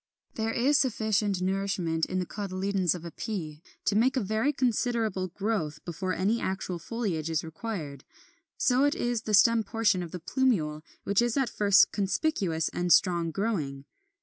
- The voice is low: No, high, 195 Hz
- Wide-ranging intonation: No, average, 4.8 semitones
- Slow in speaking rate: No, average, 175 wpm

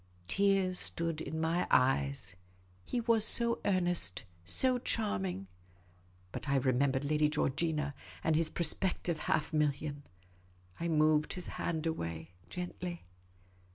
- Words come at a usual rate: No, slow, 120 wpm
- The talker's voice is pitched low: No, medium, 155 Hz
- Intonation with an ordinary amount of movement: Yes, average, 4.3 semitones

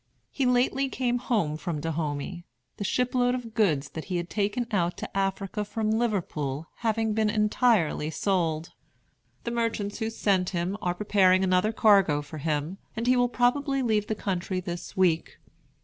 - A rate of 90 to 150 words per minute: No, average, 165 wpm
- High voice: Yes, high, 200 Hz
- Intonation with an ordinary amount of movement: Yes, average, 4.9 semitones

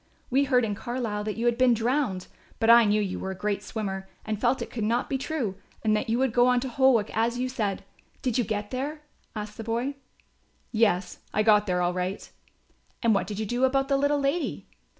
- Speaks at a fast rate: Yes, fast, 230 wpm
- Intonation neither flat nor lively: Yes, average, 3.7 semitones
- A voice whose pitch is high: Yes, high, 230 Hz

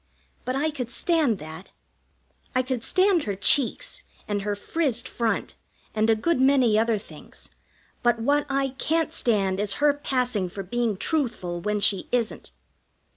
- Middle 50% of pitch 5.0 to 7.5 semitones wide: Yes, average, 5.3 semitones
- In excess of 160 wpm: No, average, 155 wpm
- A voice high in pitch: Yes, high, 240 Hz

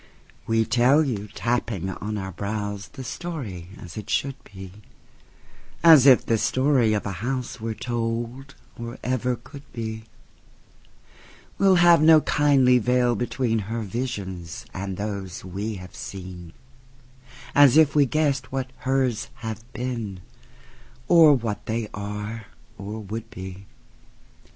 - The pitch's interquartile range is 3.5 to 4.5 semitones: Yes, average, 4.1 semitones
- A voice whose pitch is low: Yes, low, 115 Hz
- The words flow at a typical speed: No, slow, 115 wpm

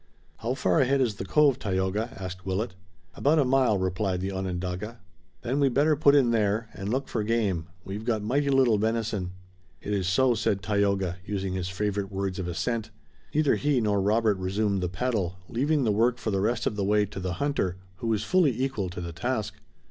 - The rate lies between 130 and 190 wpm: No, average, 200 wpm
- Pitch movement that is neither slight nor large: Yes, average, 4.4 semitones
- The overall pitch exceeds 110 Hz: No, low, 105 Hz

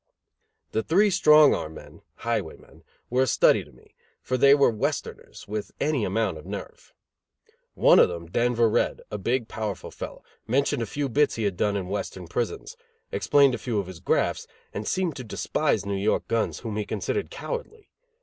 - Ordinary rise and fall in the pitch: No, wide, 5.7 semitones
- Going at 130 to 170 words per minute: No, average, 185 wpm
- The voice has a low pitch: Yes, low, 115 Hz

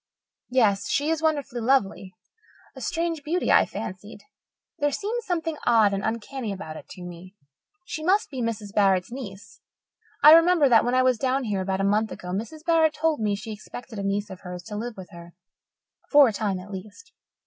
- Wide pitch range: Yes, wide, 6.8 semitones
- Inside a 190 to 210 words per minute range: Yes, average, 195 wpm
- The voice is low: No, high, 225 Hz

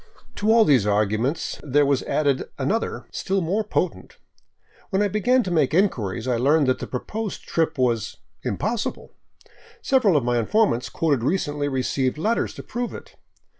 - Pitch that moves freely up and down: Yes, wide, 8.0 semitones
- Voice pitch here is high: No, medium, 150 Hz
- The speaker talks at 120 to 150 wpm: No, average, 165 wpm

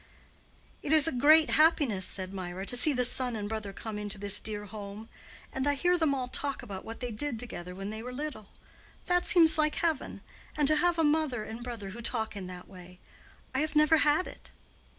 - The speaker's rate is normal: No, fast, 215 wpm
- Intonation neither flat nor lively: No, wide, 6.7 semitones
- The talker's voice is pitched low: No, high, 245 Hz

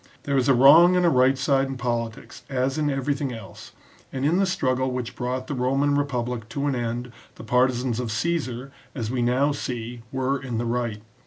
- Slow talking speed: No, average, 200 wpm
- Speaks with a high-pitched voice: No, low, 130 Hz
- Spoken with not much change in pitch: Yes, narrow, 2.3 semitones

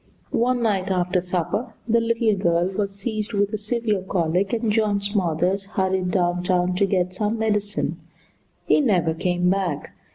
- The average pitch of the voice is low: No, high, 195 Hz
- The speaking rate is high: No, average, 160 wpm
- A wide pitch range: No, average, 3.1 semitones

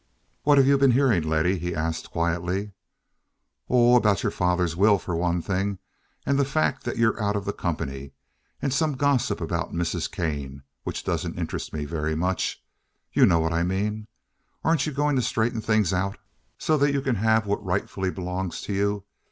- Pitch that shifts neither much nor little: No, wide, 6.0 semitones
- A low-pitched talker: Yes, low, 100 Hz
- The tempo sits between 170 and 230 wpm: Yes, average, 185 wpm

